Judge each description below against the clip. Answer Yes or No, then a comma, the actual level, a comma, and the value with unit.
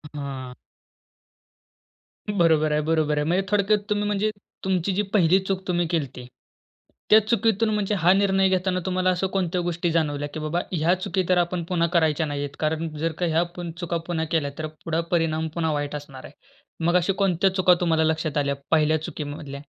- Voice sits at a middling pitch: Yes, medium, 170 Hz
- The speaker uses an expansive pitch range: No, average, 3.3 semitones